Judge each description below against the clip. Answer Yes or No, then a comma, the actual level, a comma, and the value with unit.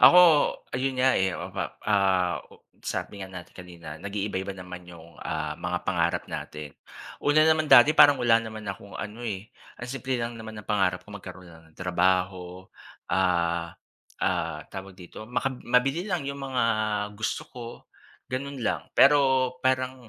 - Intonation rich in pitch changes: Yes, wide, 6.0 semitones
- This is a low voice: Yes, low, 105 Hz